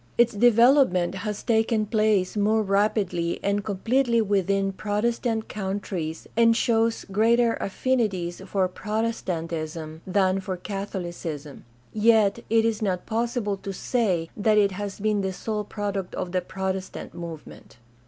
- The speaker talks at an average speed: No, slow, 130 wpm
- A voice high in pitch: Yes, high, 205 Hz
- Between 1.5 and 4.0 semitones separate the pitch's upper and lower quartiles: Yes, average, 3.1 semitones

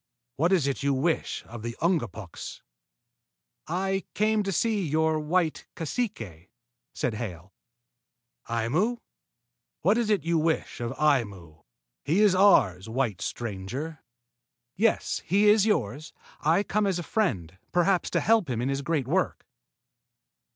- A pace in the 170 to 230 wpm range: No, slow, 135 wpm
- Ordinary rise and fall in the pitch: No, wide, 8.6 semitones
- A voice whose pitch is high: No, medium, 155 Hz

